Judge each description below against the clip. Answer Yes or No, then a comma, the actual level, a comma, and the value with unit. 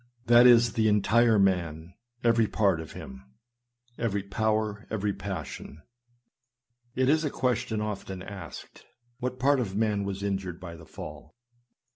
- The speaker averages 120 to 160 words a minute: Yes, average, 150 wpm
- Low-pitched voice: Yes, low, 105 Hz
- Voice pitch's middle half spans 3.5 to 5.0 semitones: Yes, average, 3.8 semitones